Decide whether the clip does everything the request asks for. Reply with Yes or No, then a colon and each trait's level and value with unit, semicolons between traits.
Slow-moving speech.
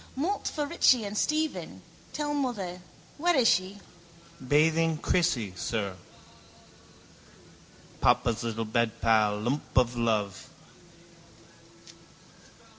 Yes: slow, 90 wpm